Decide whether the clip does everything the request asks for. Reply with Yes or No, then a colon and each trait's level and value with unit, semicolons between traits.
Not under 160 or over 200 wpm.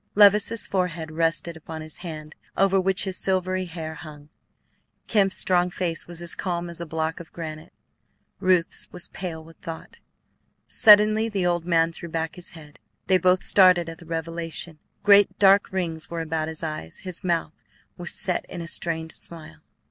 Yes: average, 170 wpm